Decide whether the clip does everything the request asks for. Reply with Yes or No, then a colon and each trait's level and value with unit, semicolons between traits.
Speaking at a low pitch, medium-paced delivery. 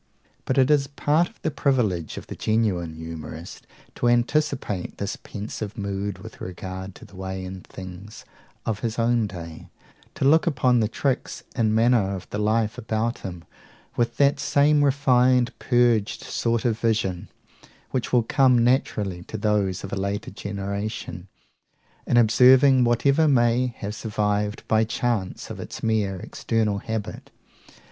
Yes: low, 110 Hz; average, 150 wpm